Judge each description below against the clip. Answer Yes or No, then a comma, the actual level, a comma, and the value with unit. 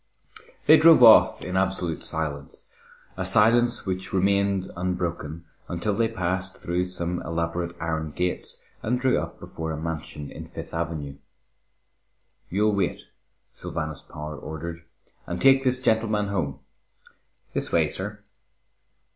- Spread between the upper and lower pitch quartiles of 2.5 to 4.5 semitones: Yes, average, 3.9 semitones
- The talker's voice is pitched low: Yes, very low, 90 Hz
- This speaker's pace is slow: Yes, slow, 130 wpm